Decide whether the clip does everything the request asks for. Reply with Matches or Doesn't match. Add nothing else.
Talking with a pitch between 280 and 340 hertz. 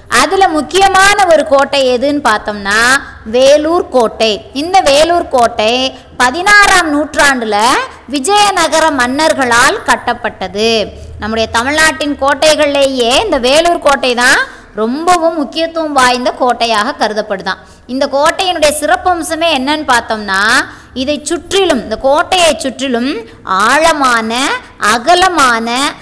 Matches